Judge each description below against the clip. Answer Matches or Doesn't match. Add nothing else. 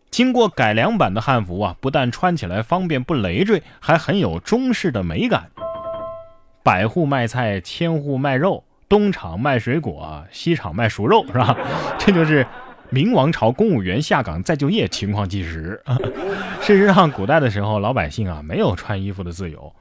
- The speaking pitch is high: Doesn't match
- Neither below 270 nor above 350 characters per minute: Doesn't match